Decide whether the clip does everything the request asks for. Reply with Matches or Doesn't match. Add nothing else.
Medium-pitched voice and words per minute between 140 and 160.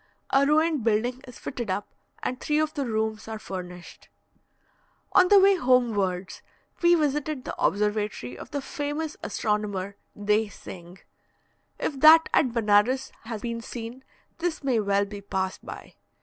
Doesn't match